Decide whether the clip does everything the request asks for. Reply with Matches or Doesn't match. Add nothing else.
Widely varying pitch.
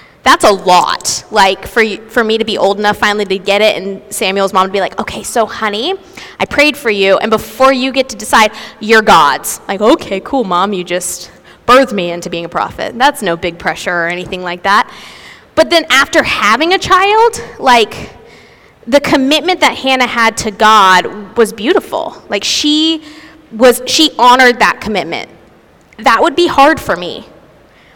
Matches